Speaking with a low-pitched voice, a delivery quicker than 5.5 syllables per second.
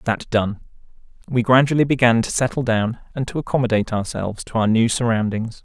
Yes: low, 120 Hz; 6.0 syllables/s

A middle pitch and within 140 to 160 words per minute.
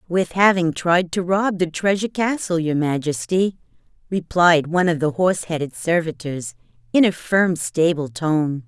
Yes: medium, 170 Hz; average, 150 wpm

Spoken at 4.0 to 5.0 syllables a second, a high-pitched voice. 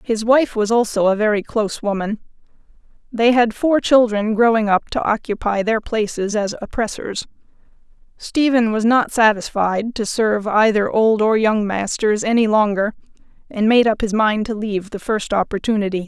Yes: 4.9 syllables/s; high, 215 Hz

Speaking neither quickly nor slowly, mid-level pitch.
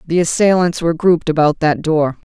Yes: average, 180 wpm; medium, 165 Hz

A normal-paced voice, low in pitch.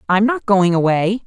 No: average, 190 wpm; high, 200 Hz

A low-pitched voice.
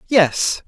No: high, 190 Hz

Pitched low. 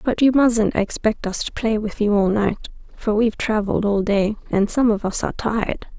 No: high, 215 Hz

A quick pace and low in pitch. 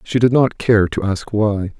Yes: fast, 235 wpm; low, 105 Hz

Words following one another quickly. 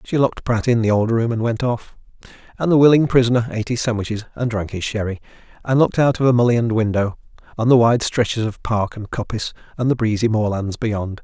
Yes: fast, 220 wpm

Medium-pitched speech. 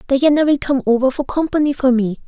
No: very high, 270 Hz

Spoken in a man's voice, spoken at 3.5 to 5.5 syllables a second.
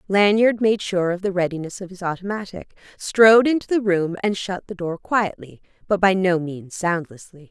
No: female; 5.0 syllables/s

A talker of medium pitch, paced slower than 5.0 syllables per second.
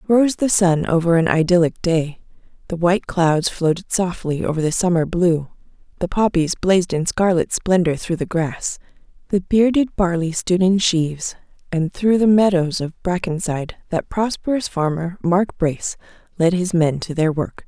Yes: medium, 175 Hz; 4.8 syllables/s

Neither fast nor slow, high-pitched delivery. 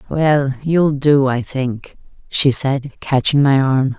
No: average, 150 wpm; low, 135 Hz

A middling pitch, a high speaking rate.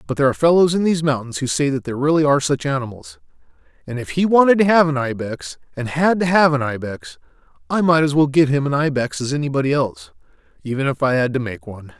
Yes: medium, 145 Hz; fast, 235 wpm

